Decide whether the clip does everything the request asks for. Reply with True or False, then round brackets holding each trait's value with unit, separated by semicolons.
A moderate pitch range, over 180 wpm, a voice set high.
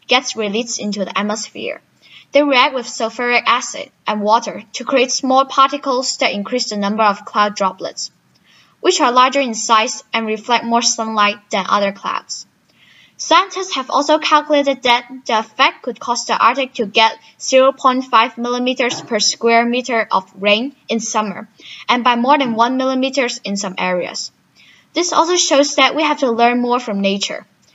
False (3.4 semitones; 165 wpm; 245 Hz)